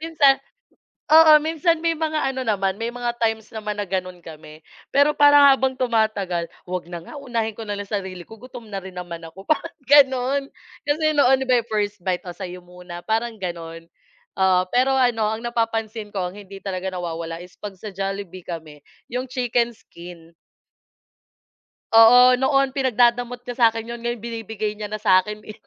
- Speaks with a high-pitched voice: Yes, high, 220 Hz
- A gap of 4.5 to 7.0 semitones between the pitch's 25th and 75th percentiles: Yes, average, 5.2 semitones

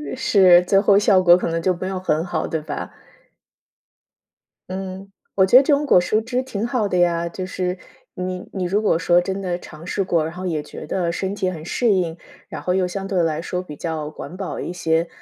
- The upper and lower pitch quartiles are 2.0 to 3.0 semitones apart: Yes, narrow, 2.4 semitones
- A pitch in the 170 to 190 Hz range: Yes, medium, 185 Hz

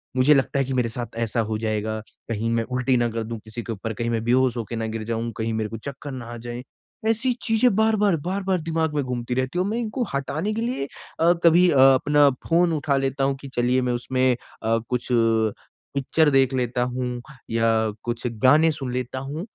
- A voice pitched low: Yes, low, 130 Hz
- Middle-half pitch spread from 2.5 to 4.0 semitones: No, average, 4.6 semitones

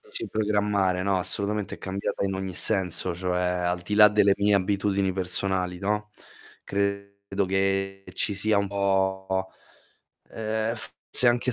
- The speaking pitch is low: Yes, low, 100 Hz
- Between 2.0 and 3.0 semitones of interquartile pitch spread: No, narrow, 1.4 semitones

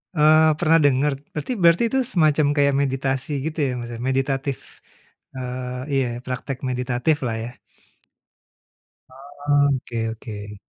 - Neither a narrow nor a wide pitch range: Yes, average, 3.2 semitones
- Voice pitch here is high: No, low, 135 Hz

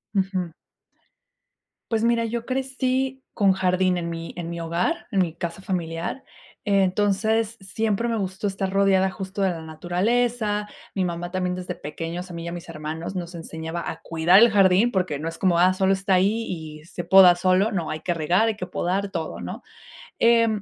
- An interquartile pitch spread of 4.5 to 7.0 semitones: No, average, 3.4 semitones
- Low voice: No, medium, 185 Hz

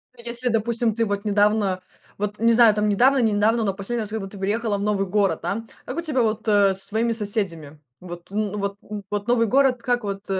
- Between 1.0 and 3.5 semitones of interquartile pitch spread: Yes, narrow, 2.5 semitones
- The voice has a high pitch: Yes, high, 210 Hz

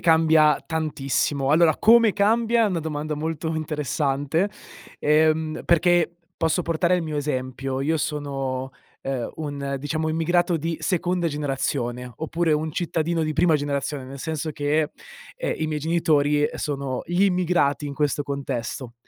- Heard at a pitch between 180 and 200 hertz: No, medium, 155 Hz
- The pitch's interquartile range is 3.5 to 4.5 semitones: No, average, 2.7 semitones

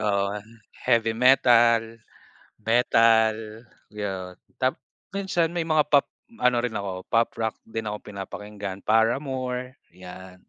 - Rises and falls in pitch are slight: No, average, 3.4 semitones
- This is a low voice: Yes, low, 110 Hz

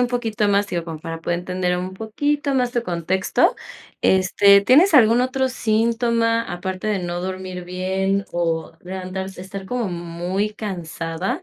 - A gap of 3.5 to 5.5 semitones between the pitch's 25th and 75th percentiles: Yes, average, 4.2 semitones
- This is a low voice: No, high, 190 Hz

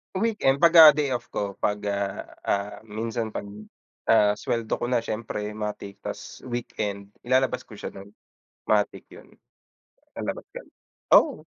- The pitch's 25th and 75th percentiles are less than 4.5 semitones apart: Yes, average, 3.5 semitones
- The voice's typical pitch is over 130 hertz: No, low, 110 Hz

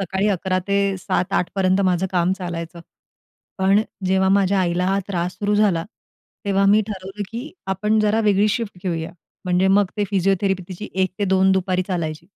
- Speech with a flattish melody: Yes, narrow, 1.7 semitones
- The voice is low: No, high, 190 Hz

